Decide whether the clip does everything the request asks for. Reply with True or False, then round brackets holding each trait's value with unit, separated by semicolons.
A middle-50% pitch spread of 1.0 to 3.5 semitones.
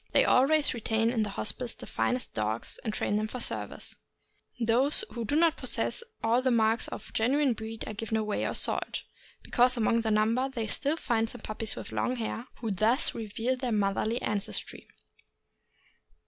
True (2.6 semitones)